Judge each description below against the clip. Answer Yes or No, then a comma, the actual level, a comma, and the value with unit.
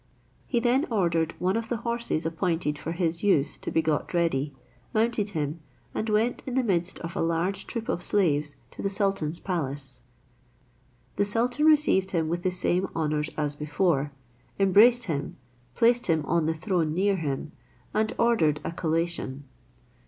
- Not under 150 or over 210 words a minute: Yes, average, 165 wpm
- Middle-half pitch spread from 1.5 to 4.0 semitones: No, average, 5.2 semitones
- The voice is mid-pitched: Yes, medium, 175 Hz